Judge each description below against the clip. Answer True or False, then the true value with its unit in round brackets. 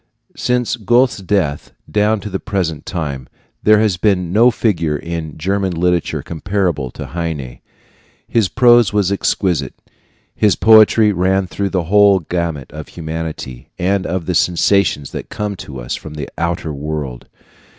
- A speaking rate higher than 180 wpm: False (150 wpm)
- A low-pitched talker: True (90 Hz)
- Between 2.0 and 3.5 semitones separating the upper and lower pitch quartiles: False (4.5 semitones)